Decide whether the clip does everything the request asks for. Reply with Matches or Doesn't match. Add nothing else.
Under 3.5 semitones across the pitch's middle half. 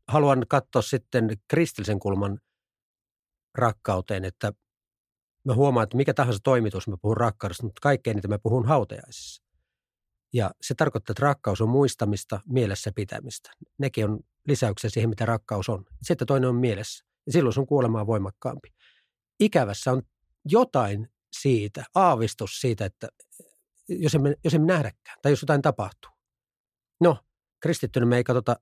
Doesn't match